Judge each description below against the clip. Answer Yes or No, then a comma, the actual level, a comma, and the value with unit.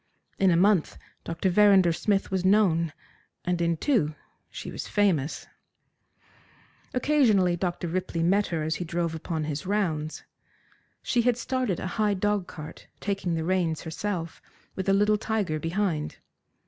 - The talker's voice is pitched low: No, medium, 185 Hz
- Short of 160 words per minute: Yes, average, 145 wpm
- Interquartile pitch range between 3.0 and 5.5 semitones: Yes, average, 3.8 semitones